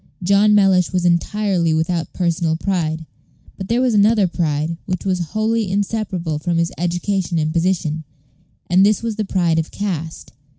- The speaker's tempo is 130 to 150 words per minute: No, average, 160 wpm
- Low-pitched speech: No, medium, 180 Hz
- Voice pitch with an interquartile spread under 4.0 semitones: Yes, average, 3.5 semitones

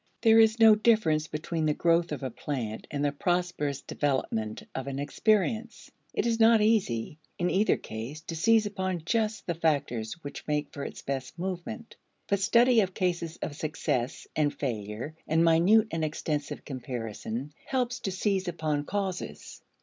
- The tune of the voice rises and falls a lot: Yes, wide, 6.3 semitones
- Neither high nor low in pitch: Yes, medium, 165 Hz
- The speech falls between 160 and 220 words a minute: Yes, average, 165 wpm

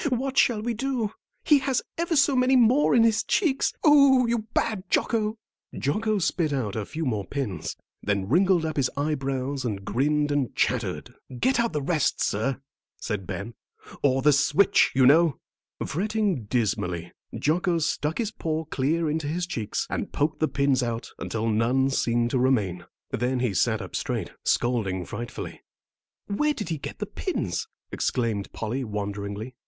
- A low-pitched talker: No, medium, 145 Hz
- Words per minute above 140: Yes, average, 165 wpm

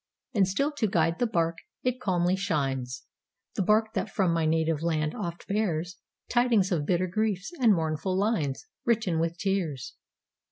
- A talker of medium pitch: Yes, medium, 180 Hz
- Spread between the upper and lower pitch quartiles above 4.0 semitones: Yes, average, 4.5 semitones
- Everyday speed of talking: Yes, average, 145 wpm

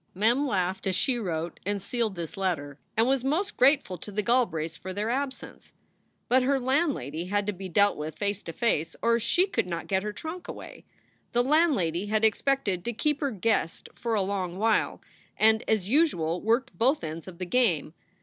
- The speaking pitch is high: Yes, high, 210 Hz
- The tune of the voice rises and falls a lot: Yes, wide, 5.9 semitones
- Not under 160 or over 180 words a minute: No, average, 195 wpm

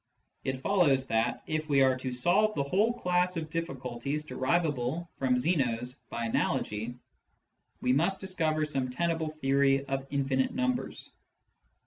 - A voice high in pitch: No, medium, 140 Hz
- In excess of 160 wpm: No, slow, 135 wpm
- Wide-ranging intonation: No, average, 4.6 semitones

